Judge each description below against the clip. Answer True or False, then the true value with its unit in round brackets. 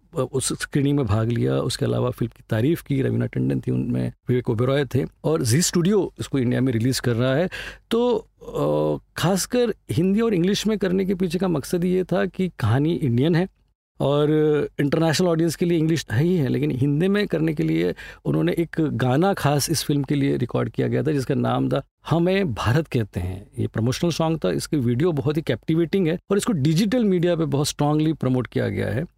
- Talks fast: True (205 wpm)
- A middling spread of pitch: False (5.9 semitones)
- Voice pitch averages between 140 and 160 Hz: True (150 Hz)